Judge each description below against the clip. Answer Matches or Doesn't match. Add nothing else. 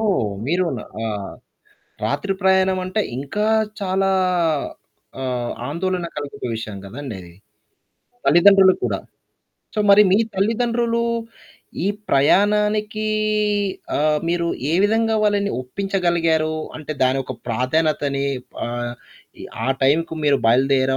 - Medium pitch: Matches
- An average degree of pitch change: Doesn't match